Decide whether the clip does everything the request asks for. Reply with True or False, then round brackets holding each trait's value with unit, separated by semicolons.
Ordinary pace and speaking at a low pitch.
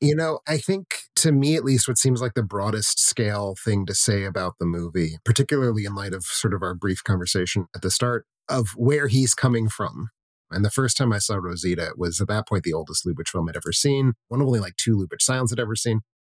False (245 wpm; 110 Hz)